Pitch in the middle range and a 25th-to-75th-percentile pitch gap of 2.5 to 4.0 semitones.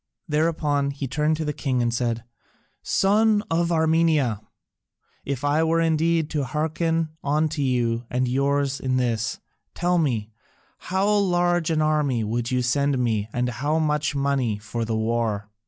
No: medium, 145 Hz; average, 4.7 semitones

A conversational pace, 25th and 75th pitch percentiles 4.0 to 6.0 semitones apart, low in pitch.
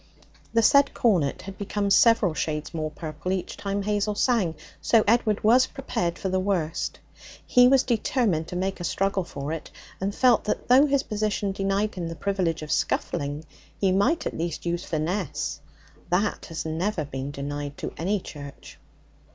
No: average, 170 wpm; average, 4.8 semitones; high, 190 Hz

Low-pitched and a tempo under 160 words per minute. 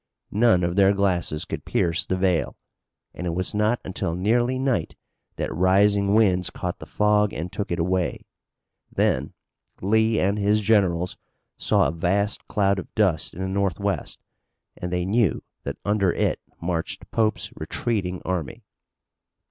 Yes: very low, 95 Hz; average, 150 wpm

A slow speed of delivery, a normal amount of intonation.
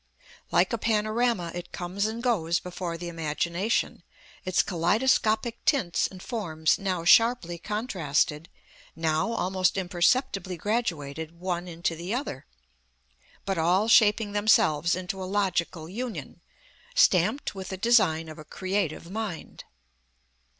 Yes: slow, 120 wpm; average, 4.3 semitones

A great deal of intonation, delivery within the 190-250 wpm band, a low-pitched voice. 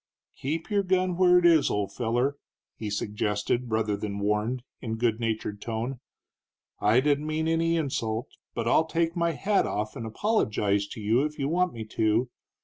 No: wide, 7.0 semitones; average, 175 wpm; low, 120 Hz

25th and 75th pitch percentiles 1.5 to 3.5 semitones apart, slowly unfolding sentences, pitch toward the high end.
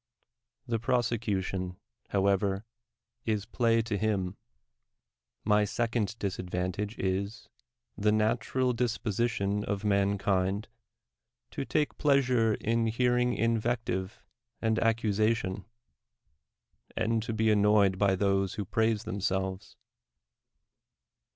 No: average, 2.7 semitones; slow, 100 wpm; low, 105 Hz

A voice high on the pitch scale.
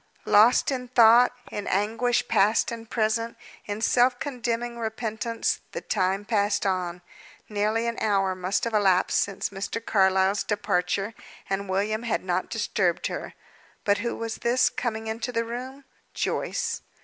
Yes: high, 220 Hz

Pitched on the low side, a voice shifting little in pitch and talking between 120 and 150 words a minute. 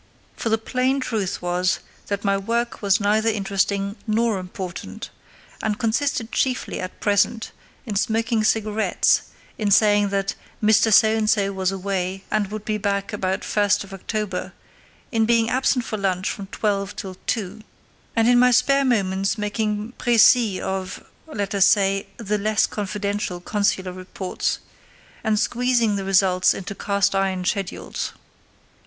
No: high, 205 Hz; narrow, 2.3 semitones; average, 140 wpm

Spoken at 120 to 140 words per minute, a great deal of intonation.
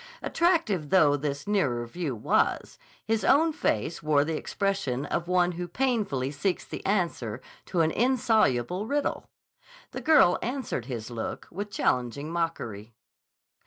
Yes: slow, 135 wpm; wide, 7.4 semitones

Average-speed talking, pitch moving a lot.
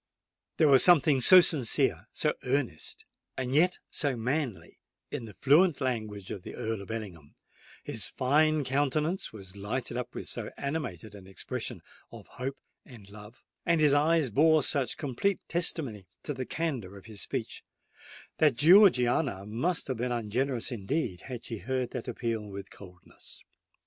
Yes: average, 145 wpm; wide, 5.9 semitones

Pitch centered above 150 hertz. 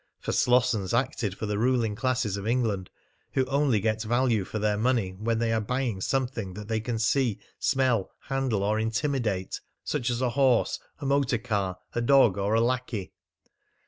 No: low, 115 Hz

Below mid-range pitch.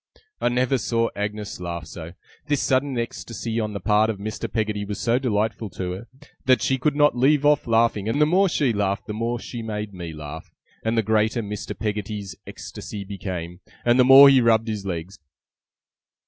Yes: low, 110 Hz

